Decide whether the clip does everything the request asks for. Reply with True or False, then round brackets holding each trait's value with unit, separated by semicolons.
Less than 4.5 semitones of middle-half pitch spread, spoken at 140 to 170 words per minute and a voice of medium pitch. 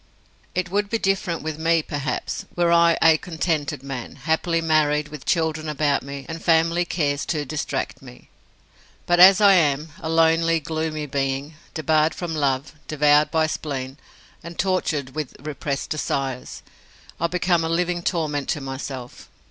True (2.7 semitones; 155 wpm; 155 Hz)